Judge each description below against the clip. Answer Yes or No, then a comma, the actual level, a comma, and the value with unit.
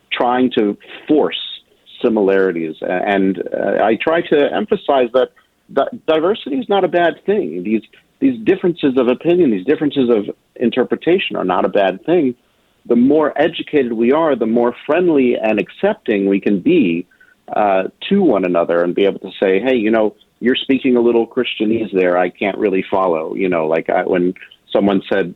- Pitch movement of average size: No, wide, 7.2 semitones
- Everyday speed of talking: Yes, average, 175 wpm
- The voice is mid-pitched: No, low, 120 Hz